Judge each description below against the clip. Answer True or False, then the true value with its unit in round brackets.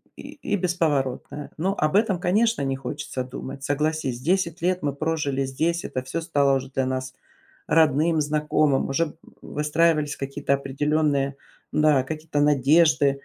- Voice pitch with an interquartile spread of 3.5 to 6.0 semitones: False (3.1 semitones)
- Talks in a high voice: False (150 Hz)